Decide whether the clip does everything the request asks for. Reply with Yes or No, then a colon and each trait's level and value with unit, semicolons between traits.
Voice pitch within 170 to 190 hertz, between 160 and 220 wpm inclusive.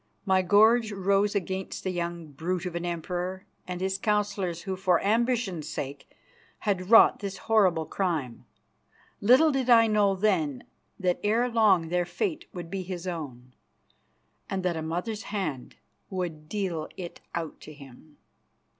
No: medium, 185 Hz; average, 150 wpm